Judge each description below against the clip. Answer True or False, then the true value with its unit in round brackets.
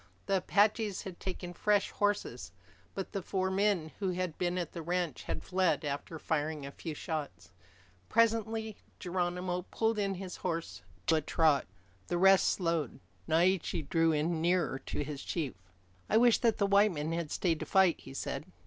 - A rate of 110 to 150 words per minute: False (175 wpm)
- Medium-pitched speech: True (175 Hz)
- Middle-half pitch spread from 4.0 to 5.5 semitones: False (3.6 semitones)